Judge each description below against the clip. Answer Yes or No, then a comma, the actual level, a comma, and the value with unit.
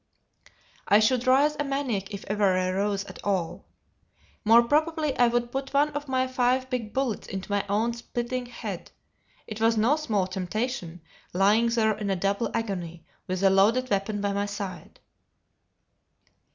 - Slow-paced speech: No, average, 165 wpm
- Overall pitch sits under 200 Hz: No, high, 220 Hz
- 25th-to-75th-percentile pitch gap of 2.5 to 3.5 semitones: No, average, 4.3 semitones